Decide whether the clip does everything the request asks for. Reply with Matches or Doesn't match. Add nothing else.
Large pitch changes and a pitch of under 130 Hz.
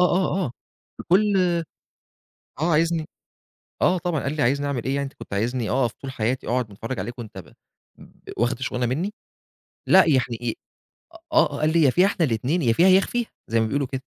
Doesn't match